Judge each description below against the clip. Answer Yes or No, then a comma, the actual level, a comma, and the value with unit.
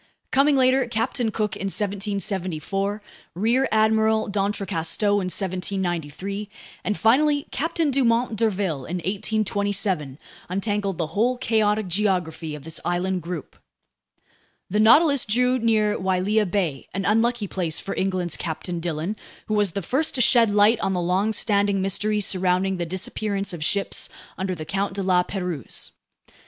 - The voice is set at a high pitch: Yes, high, 200 Hz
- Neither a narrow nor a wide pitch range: Yes, average, 3.2 semitones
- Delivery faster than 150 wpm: No, average, 140 wpm